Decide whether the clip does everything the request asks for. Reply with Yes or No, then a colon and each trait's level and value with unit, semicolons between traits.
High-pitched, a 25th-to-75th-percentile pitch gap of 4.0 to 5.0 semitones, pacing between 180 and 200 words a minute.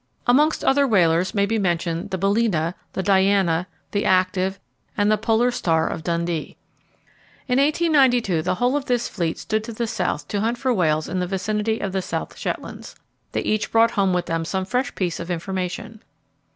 Yes: high, 195 Hz; average, 4.4 semitones; average, 185 wpm